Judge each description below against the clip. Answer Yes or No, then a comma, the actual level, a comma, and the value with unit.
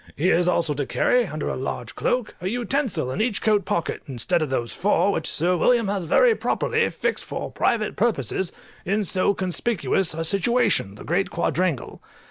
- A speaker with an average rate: Yes, average, 180 wpm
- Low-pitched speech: No, medium, 185 Hz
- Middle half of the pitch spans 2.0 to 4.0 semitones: No, wide, 5.4 semitones